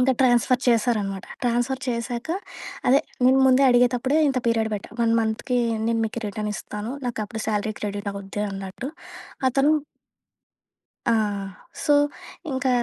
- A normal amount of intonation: Yes, average, 3.2 semitones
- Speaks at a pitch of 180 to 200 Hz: No, high, 235 Hz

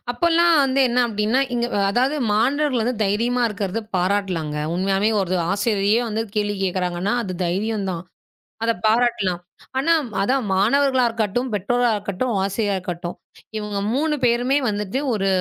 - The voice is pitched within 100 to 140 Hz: No, high, 210 Hz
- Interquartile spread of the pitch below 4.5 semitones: Yes, average, 4.0 semitones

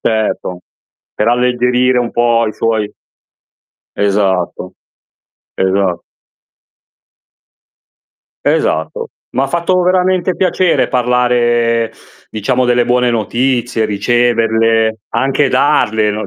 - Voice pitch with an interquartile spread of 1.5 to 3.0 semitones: Yes, narrow, 2.4 semitones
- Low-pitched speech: Yes, low, 120 Hz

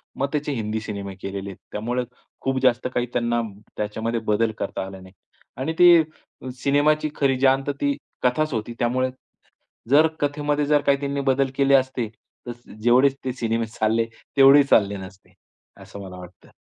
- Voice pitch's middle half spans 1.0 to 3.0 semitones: No, average, 4.3 semitones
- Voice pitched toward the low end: Yes, low, 125 Hz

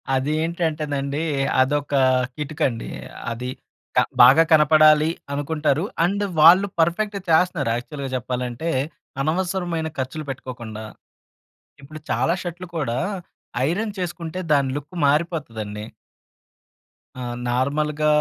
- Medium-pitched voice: Yes, medium, 150 Hz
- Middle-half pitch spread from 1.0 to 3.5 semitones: No, average, 4.0 semitones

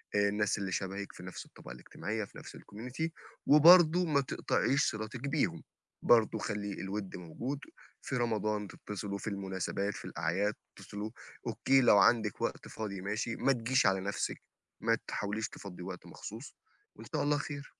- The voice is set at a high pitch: No, low, 105 Hz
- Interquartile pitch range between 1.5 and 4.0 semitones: No, average, 4.4 semitones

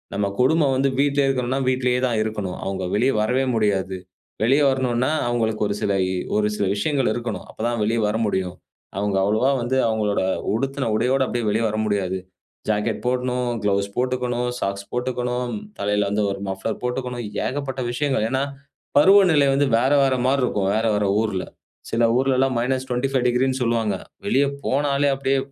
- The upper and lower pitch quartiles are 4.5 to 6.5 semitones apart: No, average, 3.8 semitones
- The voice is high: No, low, 125 Hz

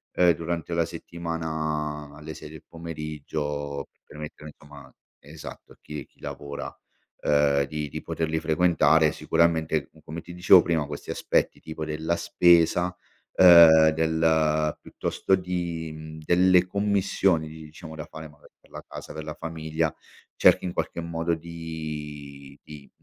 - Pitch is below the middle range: Yes, very low, 80 Hz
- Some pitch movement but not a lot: No, narrow, 1.8 semitones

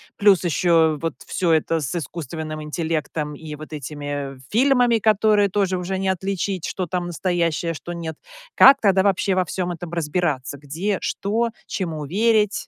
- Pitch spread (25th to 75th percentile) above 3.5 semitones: Yes, average, 4.0 semitones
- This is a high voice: No, medium, 175 Hz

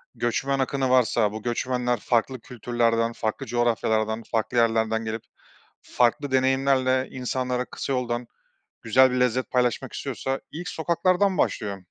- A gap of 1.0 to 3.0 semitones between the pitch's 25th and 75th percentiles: Yes, narrow, 2.4 semitones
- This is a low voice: Yes, low, 125 Hz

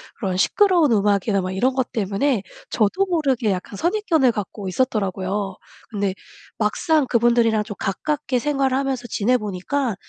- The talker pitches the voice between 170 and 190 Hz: No, high, 230 Hz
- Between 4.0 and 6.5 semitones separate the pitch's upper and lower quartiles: Yes, average, 5.3 semitones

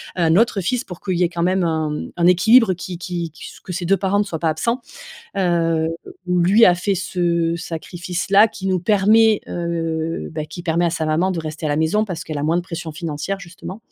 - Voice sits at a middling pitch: Yes, medium, 175 Hz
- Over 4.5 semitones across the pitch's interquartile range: No, average, 2.7 semitones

